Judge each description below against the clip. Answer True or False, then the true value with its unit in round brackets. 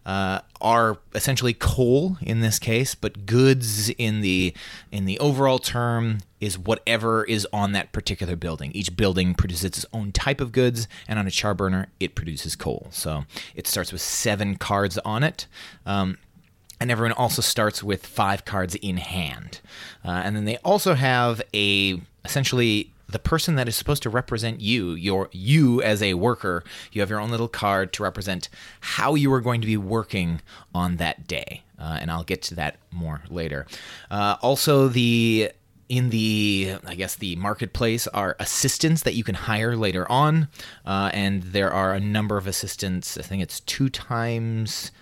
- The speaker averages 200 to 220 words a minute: False (175 wpm)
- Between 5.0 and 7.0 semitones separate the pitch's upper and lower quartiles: False (3.7 semitones)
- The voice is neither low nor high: False (105 Hz)